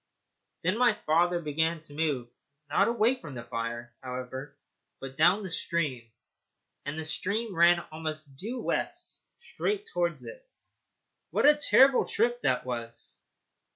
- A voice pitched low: No, medium, 160 Hz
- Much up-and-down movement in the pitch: Yes, wide, 8.1 semitones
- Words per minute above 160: No, average, 140 wpm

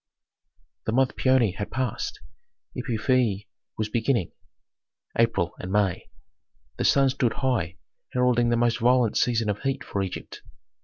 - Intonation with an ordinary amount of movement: Yes, average, 3.5 semitones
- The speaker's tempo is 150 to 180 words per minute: No, slow, 135 wpm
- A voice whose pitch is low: Yes, low, 115 Hz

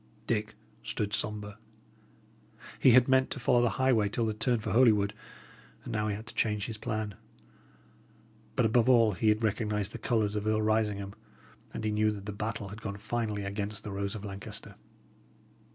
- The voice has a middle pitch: No, low, 110 Hz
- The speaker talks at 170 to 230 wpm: Yes, average, 185 wpm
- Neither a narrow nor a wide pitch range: No, narrow, 1.6 semitones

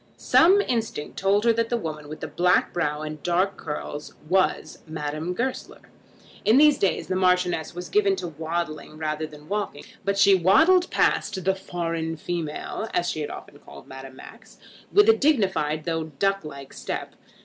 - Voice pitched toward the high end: No, medium, 175 Hz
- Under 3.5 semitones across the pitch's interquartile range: No, average, 4.5 semitones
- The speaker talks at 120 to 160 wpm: No, average, 180 wpm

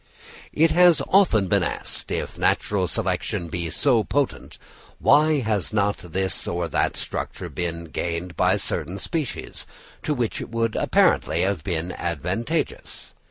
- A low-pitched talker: Yes, low, 100 Hz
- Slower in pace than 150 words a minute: Yes, average, 140 wpm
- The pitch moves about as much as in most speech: No, wide, 7.5 semitones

